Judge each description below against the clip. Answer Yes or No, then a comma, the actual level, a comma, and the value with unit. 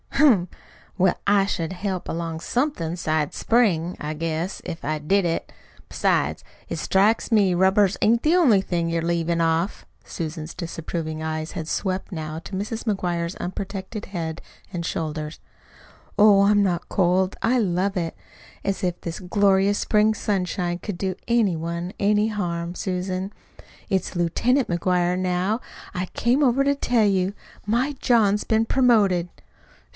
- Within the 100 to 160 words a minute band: Yes, average, 150 wpm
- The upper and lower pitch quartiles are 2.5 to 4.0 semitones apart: Yes, average, 3.5 semitones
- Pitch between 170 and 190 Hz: Yes, medium, 185 Hz